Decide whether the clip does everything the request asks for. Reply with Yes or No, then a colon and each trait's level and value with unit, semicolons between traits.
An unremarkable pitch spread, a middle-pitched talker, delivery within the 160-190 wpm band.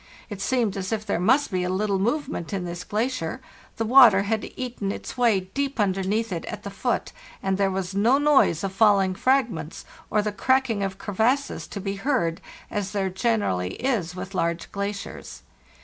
No: average, 3.8 semitones; high, 200 Hz; average, 180 wpm